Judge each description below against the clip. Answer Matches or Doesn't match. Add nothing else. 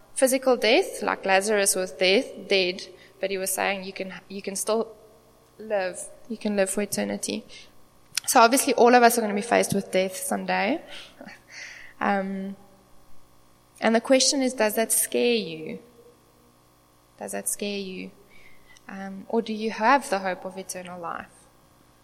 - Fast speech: Doesn't match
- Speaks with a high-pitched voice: Matches